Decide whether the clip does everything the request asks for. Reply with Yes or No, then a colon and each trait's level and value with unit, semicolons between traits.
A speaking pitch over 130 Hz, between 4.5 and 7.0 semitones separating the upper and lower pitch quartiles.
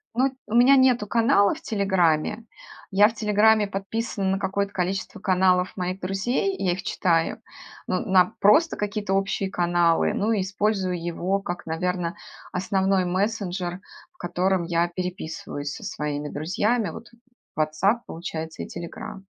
No: high, 190 Hz; average, 2.9 semitones